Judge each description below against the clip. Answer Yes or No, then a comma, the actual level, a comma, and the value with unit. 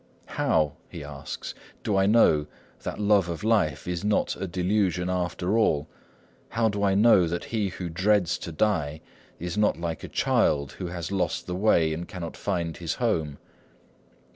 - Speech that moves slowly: No, average, 170 wpm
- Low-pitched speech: Yes, very low, 90 Hz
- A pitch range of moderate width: Yes, average, 3.9 semitones